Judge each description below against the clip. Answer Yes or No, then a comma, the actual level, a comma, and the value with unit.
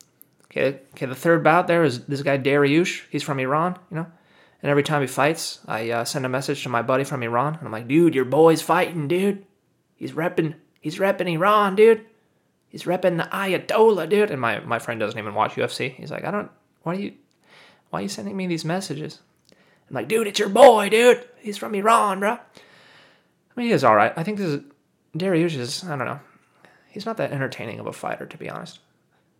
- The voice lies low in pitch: No, medium, 165 Hz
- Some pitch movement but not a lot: No, wide, 5.7 semitones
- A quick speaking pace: Yes, fast, 220 wpm